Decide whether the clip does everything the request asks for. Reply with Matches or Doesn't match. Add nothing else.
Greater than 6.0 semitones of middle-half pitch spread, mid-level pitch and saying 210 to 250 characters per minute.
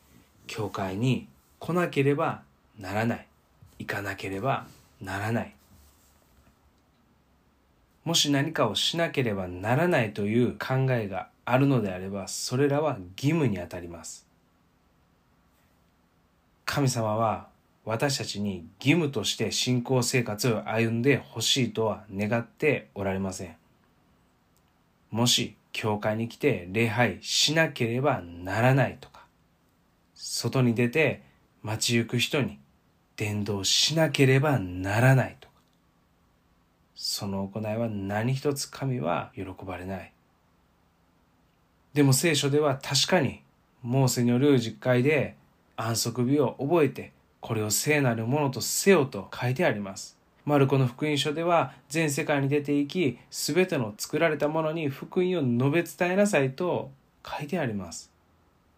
Doesn't match